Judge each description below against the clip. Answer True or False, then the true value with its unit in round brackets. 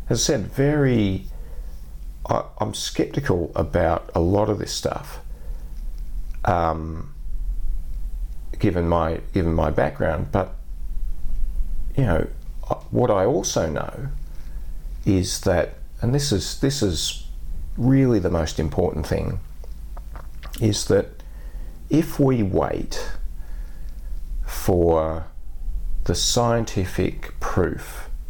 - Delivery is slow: True (100 wpm)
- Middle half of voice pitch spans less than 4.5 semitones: False (5.2 semitones)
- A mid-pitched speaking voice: False (80 Hz)